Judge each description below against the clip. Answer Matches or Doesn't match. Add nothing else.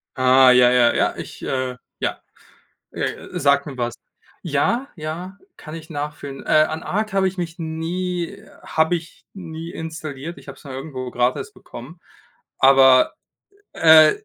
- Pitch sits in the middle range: Matches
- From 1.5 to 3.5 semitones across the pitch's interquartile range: Doesn't match